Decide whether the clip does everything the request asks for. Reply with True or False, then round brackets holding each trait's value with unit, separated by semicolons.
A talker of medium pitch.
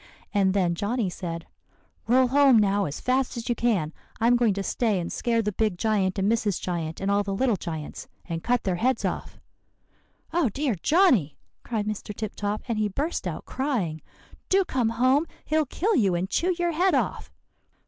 False (220 Hz)